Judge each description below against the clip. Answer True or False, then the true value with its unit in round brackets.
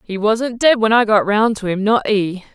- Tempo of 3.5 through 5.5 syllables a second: True (4.6 syllables/s)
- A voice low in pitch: False (215 Hz)